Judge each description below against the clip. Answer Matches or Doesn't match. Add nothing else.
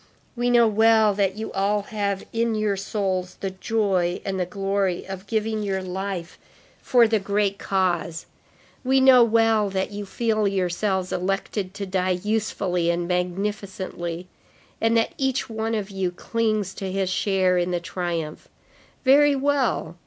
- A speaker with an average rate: Matches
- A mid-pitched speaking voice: Doesn't match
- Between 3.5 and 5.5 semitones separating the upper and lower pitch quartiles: Doesn't match